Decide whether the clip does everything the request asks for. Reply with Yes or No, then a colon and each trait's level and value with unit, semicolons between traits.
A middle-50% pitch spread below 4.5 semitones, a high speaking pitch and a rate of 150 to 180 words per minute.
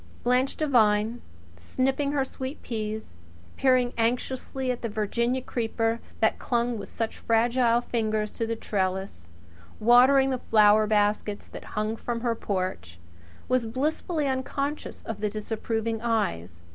No: average, 3.0 semitones; high, 230 Hz; slow, 135 wpm